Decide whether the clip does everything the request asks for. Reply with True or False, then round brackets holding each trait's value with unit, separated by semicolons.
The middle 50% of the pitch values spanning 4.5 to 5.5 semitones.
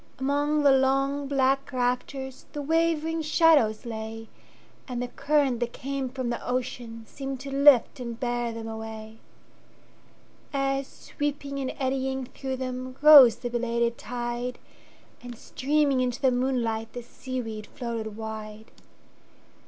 False (2.8 semitones)